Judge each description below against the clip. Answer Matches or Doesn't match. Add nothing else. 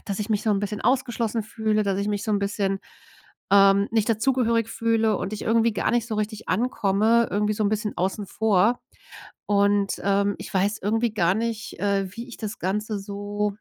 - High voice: Matches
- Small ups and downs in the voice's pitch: Matches